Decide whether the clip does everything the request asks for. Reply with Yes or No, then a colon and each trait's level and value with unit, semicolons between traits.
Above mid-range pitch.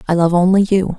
No: medium, 180 Hz